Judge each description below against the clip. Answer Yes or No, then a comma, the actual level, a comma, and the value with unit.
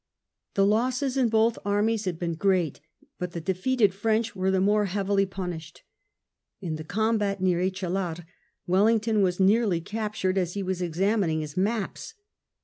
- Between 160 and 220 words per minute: No, average, 150 wpm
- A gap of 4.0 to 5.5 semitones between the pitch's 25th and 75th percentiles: No, average, 3.3 semitones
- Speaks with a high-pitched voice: Yes, high, 195 Hz